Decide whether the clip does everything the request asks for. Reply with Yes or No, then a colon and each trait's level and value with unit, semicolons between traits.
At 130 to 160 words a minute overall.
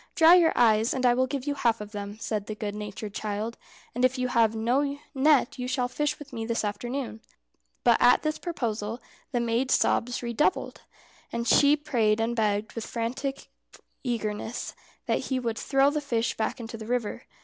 No: average, 190 wpm